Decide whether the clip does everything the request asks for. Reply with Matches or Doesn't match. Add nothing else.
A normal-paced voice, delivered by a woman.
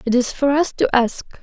Doesn't match